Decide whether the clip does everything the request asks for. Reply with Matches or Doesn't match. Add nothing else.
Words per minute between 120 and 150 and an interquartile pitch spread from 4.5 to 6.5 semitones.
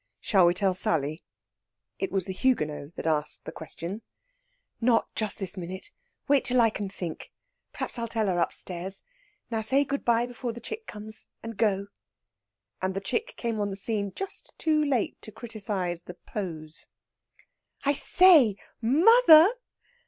Doesn't match